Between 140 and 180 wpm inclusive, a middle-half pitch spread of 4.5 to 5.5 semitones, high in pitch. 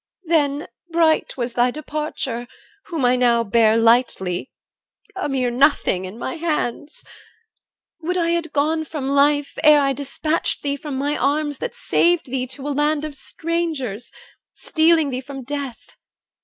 No: average, 150 wpm; average, 3.8 semitones; very high, 285 Hz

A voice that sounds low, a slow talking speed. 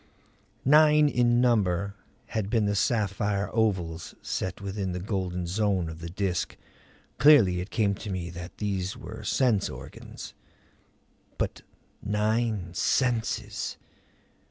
Yes: low, 100 Hz; slow, 120 wpm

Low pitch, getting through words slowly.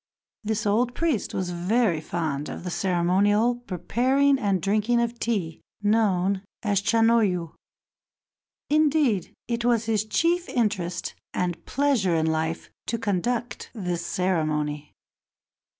No: high, 205 Hz; slow, 120 wpm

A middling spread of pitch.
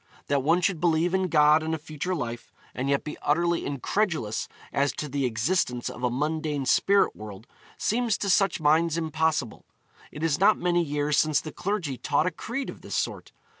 Yes: average, 3.9 semitones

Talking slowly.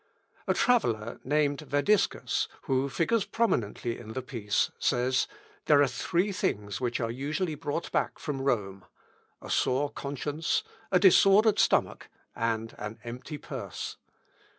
Yes: slow, 130 wpm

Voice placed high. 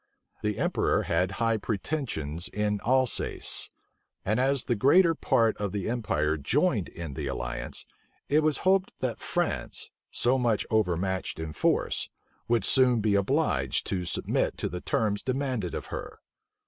No: low, 110 Hz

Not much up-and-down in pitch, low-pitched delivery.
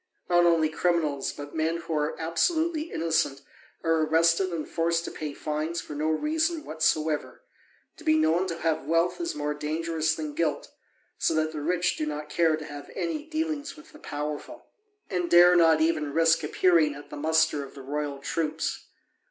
No: narrow, 2.1 semitones; medium, 160 Hz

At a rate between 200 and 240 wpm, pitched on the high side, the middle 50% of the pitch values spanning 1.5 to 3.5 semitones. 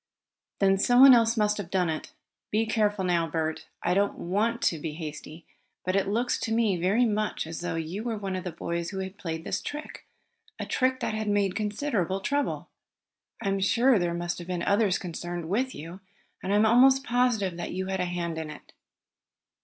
No: fast, 205 wpm; high, 195 Hz; average, 4.2 semitones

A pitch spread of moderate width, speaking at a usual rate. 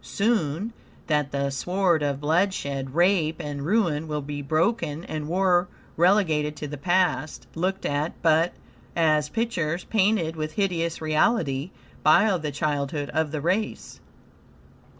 No: average, 3.8 semitones; slow, 130 wpm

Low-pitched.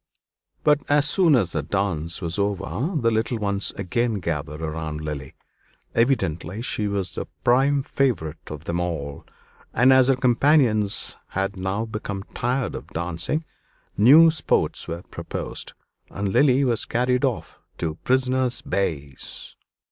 Yes: low, 105 Hz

